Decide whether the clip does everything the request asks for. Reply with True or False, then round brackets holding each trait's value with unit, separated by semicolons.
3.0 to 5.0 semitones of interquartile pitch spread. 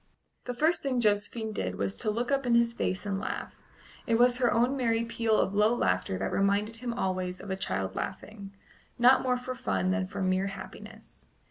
True (4.3 semitones)